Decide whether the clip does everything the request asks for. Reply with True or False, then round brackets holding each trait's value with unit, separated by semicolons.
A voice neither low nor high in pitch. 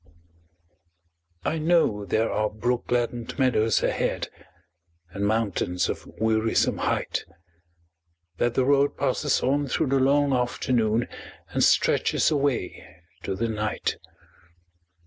False (120 Hz)